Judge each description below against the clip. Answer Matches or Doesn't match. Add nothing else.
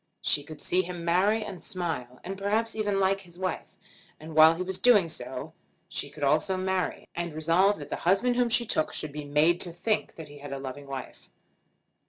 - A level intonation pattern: Doesn't match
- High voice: Doesn't match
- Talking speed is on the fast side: Matches